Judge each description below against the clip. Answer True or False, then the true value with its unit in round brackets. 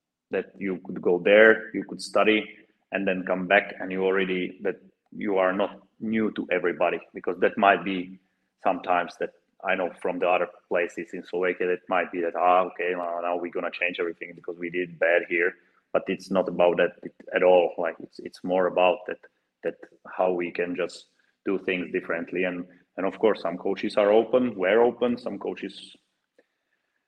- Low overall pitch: True (95 Hz)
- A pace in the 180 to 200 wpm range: True (195 wpm)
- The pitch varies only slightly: True (2.3 semitones)